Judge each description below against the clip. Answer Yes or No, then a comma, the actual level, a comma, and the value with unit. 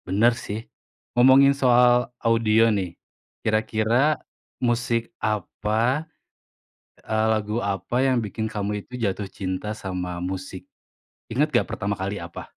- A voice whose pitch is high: No, low, 110 Hz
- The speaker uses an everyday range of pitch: Yes, average, 3.4 semitones